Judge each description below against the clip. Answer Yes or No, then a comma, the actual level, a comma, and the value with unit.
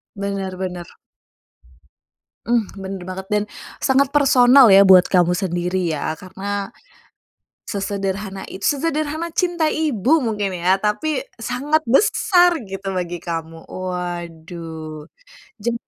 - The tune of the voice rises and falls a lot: Yes, wide, 6.3 semitones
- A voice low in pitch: No, high, 195 Hz